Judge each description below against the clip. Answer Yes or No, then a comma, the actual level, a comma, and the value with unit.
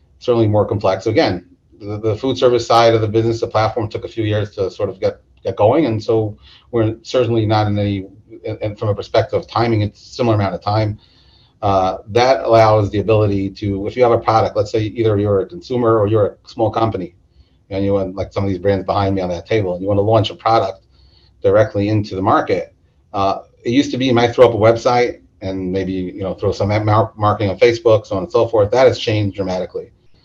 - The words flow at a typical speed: No, fast, 230 wpm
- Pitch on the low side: Yes, low, 105 Hz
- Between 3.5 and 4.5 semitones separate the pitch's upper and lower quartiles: No, average, 2.7 semitones